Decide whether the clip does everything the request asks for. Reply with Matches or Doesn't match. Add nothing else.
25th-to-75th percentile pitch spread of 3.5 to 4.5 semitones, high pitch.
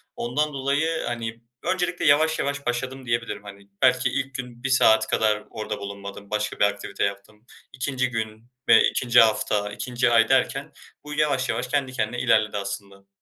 Doesn't match